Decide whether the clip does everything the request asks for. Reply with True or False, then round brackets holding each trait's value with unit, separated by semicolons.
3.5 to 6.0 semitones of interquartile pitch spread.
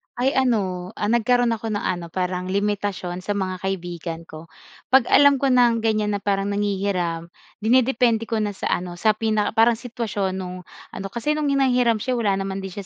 True (4.0 semitones)